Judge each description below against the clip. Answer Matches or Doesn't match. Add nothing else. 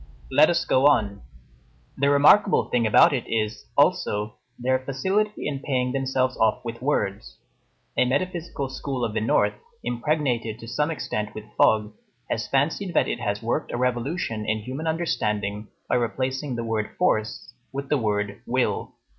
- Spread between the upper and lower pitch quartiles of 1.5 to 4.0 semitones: Doesn't match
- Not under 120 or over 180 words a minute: Matches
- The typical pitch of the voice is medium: Doesn't match